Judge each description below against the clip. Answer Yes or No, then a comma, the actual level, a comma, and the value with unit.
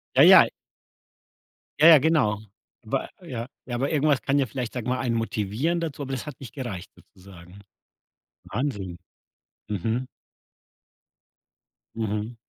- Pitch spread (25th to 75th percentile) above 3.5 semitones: Yes, average, 4.8 semitones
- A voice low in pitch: Yes, low, 120 Hz